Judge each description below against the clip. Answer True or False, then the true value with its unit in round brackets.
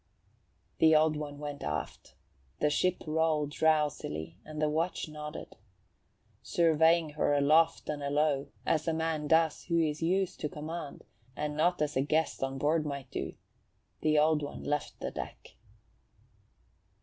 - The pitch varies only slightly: True (1.6 semitones)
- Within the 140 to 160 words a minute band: True (150 wpm)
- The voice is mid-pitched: True (150 Hz)